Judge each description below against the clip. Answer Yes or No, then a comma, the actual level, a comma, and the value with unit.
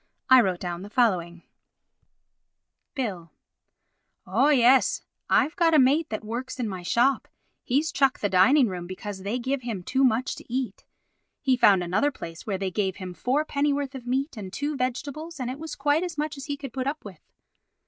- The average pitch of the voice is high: Yes, very high, 250 Hz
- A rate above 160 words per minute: Yes, average, 190 wpm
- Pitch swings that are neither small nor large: No, wide, 6.3 semitones